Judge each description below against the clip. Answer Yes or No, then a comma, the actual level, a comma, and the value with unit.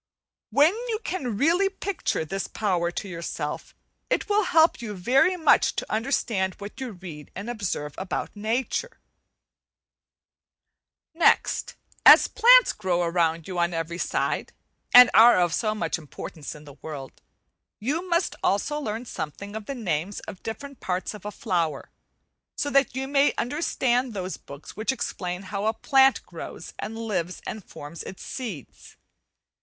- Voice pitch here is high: Yes, high, 210 Hz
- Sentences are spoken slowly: No, average, 155 wpm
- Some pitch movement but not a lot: No, wide, 7.1 semitones